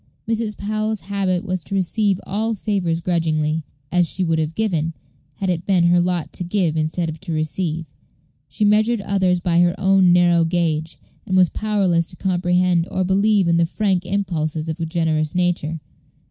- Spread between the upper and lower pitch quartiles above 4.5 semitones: No, average, 2.9 semitones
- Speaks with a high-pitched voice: No, medium, 180 Hz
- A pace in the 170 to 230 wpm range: Yes, average, 175 wpm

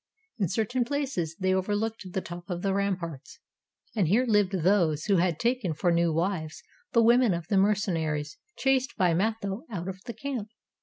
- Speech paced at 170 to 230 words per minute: Yes, average, 175 wpm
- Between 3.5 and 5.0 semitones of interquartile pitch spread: Yes, average, 4.4 semitones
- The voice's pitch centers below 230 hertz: Yes, high, 190 Hz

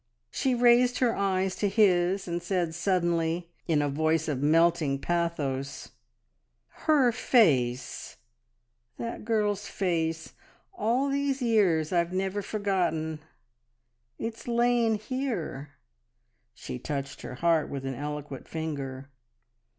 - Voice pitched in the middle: Yes, medium, 175 Hz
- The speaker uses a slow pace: Yes, slow, 110 wpm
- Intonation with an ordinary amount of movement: No, wide, 6.1 semitones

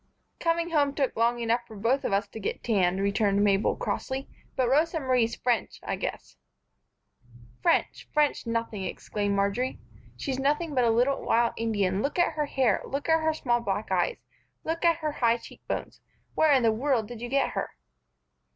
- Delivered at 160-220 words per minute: Yes, average, 180 wpm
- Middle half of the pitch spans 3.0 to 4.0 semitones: No, average, 4.7 semitones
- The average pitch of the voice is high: Yes, high, 240 Hz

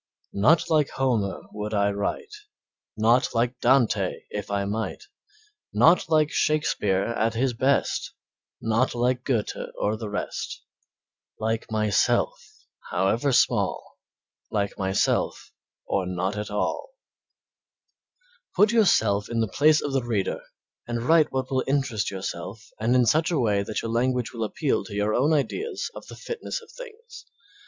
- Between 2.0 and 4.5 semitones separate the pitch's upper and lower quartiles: No, wide, 5.5 semitones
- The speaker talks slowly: No, average, 145 wpm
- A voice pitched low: Yes, low, 115 Hz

